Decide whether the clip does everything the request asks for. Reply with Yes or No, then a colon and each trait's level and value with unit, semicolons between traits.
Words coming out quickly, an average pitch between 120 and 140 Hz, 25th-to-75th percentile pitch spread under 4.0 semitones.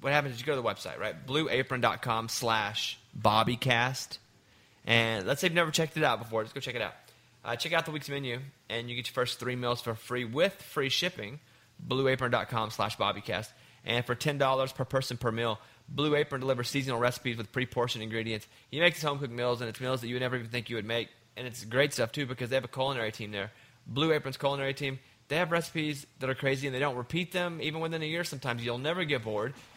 Yes: fast, 230 wpm; low, 125 Hz; average, 3.3 semitones